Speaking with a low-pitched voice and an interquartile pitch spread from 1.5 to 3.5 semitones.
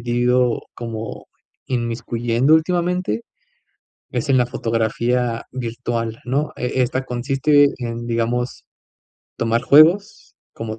Yes: low, 120 Hz; narrow, 2.4 semitones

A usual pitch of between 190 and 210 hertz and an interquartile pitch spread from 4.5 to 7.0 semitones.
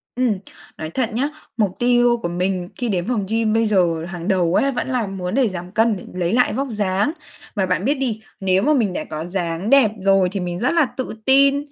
Yes: high, 205 Hz; average, 5.2 semitones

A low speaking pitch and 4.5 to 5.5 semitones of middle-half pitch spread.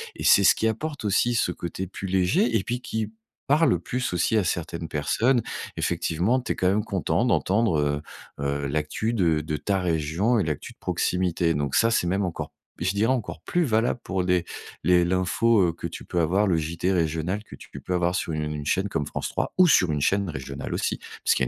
Yes: very low, 90 Hz; average, 5.1 semitones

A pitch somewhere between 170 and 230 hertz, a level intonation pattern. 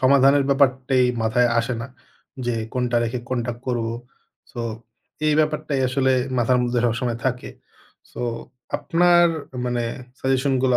No: low, 130 Hz; narrow, 2.1 semitones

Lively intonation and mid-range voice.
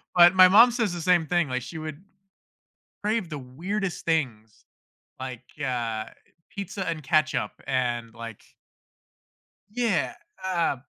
Yes: wide, 6.6 semitones; medium, 160 Hz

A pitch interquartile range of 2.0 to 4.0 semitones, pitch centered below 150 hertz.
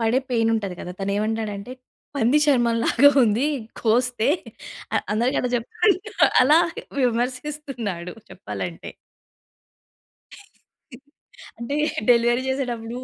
No: average, 2.8 semitones; high, 240 Hz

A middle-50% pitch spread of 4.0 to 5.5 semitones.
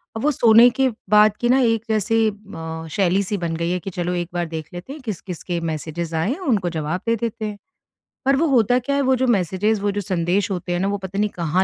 Yes: average, 4.7 semitones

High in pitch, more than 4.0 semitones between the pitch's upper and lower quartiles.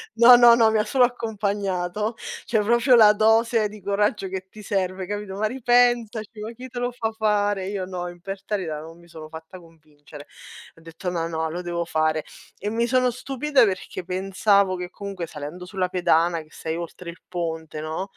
Yes: high, 195 Hz; average, 4.4 semitones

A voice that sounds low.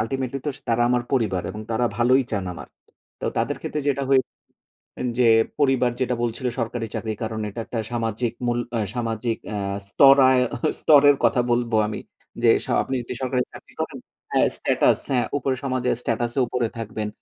Yes: low, 120 Hz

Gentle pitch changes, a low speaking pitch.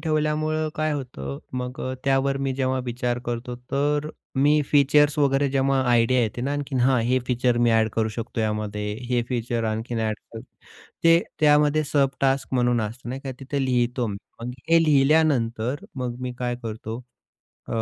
No: average, 3.2 semitones; low, 130 Hz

